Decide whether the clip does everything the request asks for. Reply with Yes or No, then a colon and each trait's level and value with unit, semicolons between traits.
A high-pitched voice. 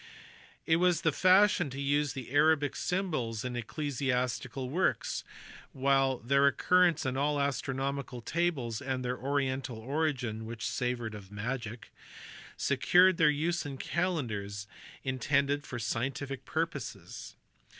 No: low, 135 Hz